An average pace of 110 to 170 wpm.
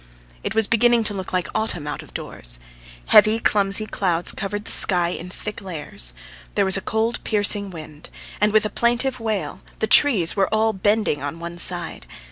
No: average, 185 wpm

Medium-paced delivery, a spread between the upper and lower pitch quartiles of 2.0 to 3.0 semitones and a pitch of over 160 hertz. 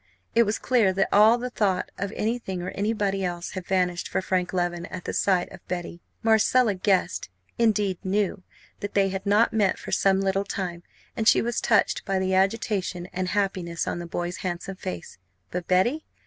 Yes: average, 185 wpm; narrow, 2.4 semitones; high, 190 Hz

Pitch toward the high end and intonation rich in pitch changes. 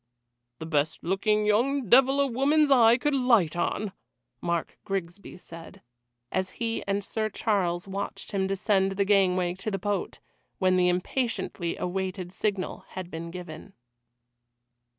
No: high, 195 Hz; average, 3.7 semitones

